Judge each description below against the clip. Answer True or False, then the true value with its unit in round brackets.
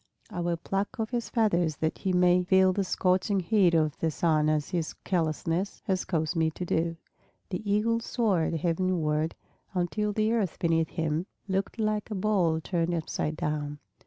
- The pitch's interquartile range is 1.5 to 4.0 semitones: True (3.6 semitones)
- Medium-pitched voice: True (175 Hz)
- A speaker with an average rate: True (170 wpm)